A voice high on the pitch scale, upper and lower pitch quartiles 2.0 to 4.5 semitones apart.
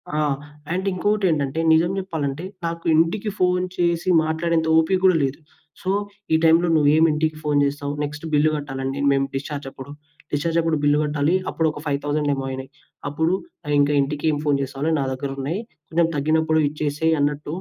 No: medium, 150 Hz; narrow, 2.5 semitones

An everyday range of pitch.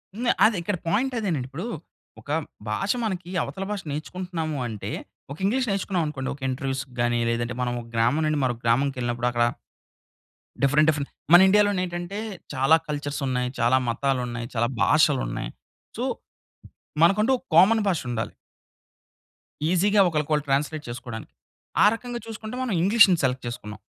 No: wide, 7.3 semitones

